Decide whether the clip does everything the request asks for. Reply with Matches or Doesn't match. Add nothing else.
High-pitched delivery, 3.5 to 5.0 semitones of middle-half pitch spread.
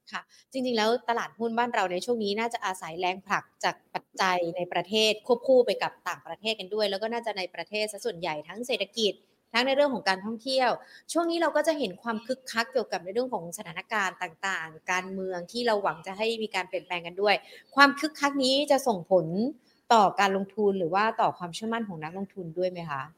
Matches